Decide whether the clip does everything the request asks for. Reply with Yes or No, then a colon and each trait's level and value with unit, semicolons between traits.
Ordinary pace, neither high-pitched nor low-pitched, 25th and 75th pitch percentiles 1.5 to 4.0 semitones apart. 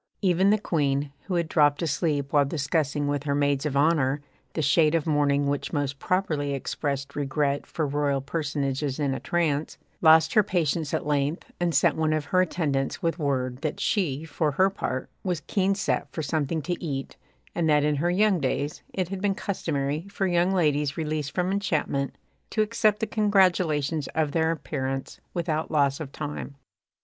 Yes: average, 180 wpm; medium, 150 Hz; average, 3.4 semitones